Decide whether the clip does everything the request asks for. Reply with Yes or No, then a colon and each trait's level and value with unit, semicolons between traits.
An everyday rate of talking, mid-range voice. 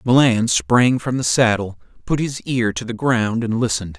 No: average, 195 wpm; low, 115 Hz